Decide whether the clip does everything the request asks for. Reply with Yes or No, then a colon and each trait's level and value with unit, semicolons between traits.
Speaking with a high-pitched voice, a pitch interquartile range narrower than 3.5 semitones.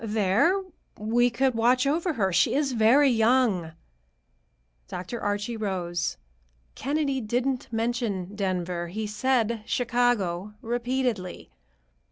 No: high, 230 Hz; average, 4.1 semitones